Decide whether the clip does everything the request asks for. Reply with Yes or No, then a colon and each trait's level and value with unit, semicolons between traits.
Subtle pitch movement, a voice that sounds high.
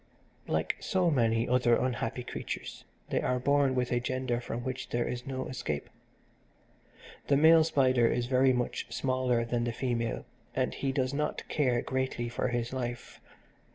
No: narrow, 1.6 semitones; low, 125 Hz